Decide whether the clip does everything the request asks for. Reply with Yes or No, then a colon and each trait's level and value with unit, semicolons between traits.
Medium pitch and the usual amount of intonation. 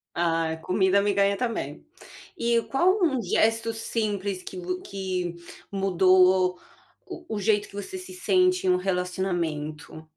No: high, 195 Hz; average, 3.9 semitones